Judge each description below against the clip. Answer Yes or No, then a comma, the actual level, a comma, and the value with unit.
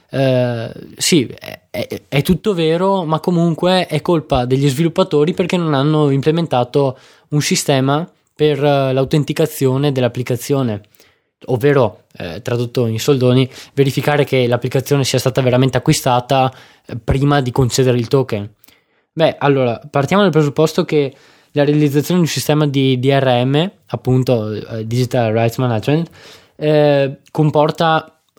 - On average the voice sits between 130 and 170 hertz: Yes, medium, 140 Hz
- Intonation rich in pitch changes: No, average, 3.3 semitones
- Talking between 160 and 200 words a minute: No, average, 120 wpm